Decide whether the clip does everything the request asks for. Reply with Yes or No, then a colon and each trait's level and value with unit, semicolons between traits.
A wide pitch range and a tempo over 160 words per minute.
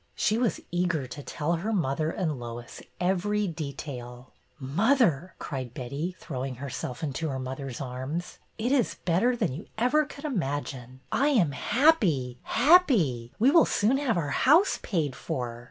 No: wide, 9.0 semitones; average, 155 wpm